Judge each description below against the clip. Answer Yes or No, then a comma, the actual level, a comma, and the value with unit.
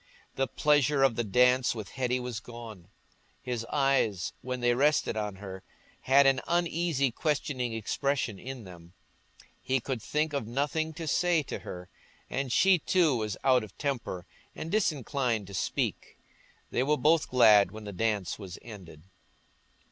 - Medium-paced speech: Yes, average, 155 wpm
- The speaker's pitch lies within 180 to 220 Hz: No, low, 125 Hz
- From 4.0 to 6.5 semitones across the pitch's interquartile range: Yes, average, 4.9 semitones